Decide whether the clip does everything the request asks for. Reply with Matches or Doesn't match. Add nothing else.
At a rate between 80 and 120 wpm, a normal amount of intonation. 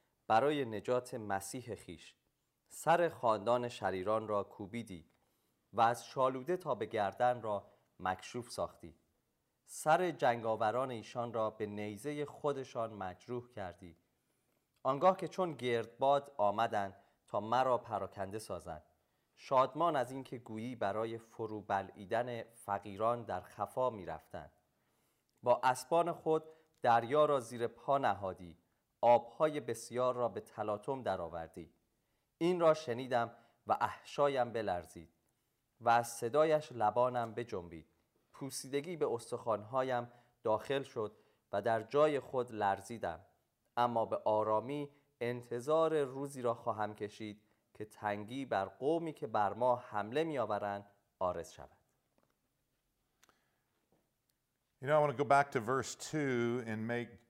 Matches